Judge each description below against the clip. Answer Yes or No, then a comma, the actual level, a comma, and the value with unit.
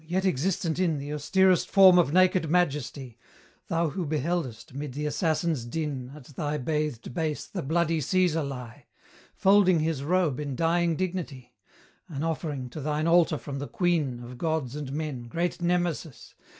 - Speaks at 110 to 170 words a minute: Yes, average, 160 wpm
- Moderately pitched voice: Yes, medium, 155 Hz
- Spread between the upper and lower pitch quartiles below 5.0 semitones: Yes, average, 3.8 semitones